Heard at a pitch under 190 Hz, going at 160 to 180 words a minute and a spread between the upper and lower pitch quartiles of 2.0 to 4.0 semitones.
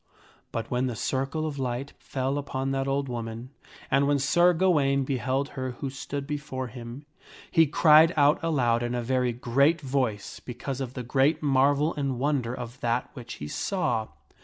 Yes: low, 135 Hz; average, 175 wpm; narrow, 2.6 semitones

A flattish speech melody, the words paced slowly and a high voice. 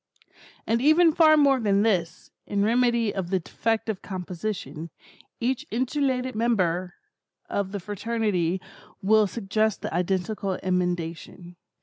No: average, 4.4 semitones; slow, 115 wpm; high, 205 Hz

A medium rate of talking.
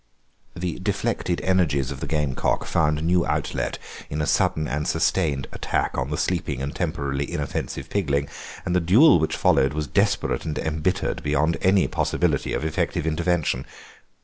Yes: average, 155 wpm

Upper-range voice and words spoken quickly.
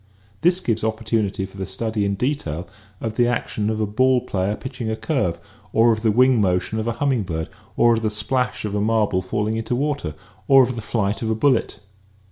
No: low, 110 Hz; fast, 220 wpm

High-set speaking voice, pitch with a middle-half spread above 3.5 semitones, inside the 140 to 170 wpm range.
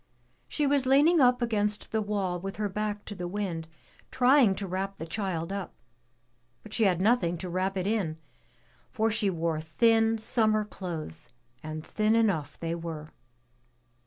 Yes: high, 200 Hz; average, 4.5 semitones; average, 160 wpm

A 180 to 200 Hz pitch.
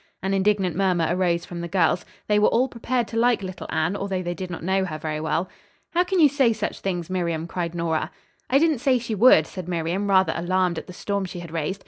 Yes: medium, 185 Hz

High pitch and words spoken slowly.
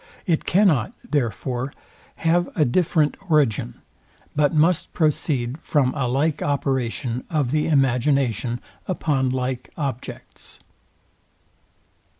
No: medium, 140 Hz; slow, 100 wpm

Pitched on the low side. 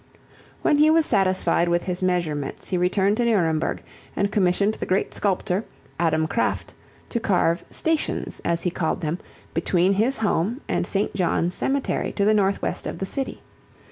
No: high, 190 Hz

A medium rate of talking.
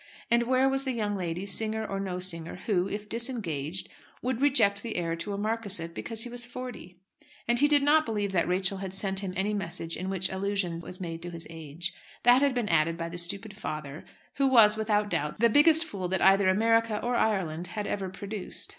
No: fast, 215 wpm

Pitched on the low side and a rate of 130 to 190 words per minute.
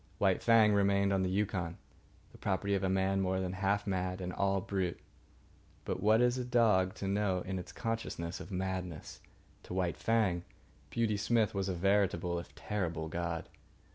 Yes: very low, 95 Hz; average, 175 wpm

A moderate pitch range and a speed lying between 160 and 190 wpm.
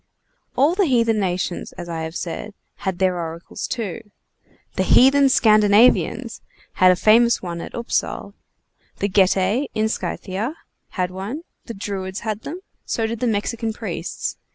No: average, 4.0 semitones; average, 150 wpm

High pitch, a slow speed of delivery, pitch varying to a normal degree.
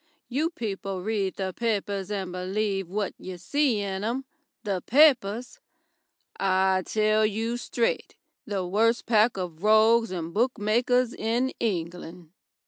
Yes: high, 210 Hz; slow, 130 wpm; average, 3.5 semitones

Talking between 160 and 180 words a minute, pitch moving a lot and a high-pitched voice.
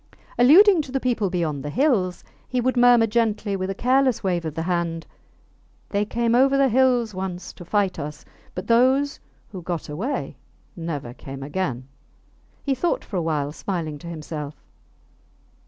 Yes: average, 165 wpm; wide, 7.1 semitones; high, 195 Hz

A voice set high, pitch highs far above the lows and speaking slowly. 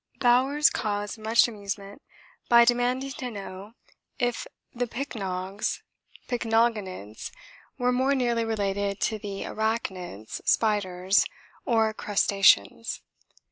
No: high, 220 Hz; average, 3.6 semitones; slow, 100 wpm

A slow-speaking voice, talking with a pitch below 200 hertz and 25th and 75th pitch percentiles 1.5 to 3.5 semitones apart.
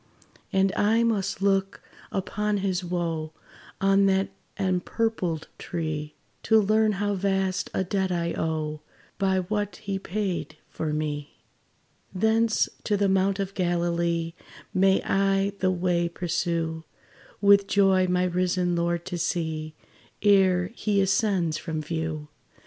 Yes: slow, 125 wpm; medium, 185 Hz; narrow, 2.6 semitones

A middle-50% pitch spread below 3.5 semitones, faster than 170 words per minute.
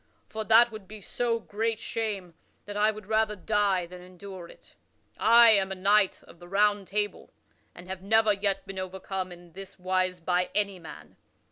Yes: narrow, 2.6 semitones; average, 180 wpm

